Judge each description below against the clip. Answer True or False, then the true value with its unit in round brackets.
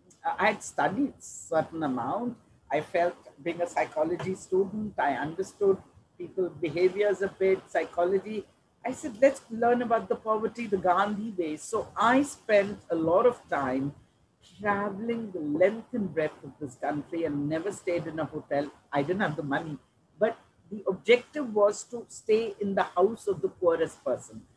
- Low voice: False (195 Hz)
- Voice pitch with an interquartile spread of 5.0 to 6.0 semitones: True (5.3 semitones)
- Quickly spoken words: False (165 wpm)